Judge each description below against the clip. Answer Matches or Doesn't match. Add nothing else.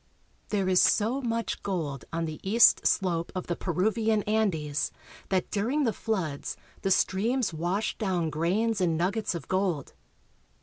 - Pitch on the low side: Doesn't match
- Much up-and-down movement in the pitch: Doesn't match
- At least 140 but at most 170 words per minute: Matches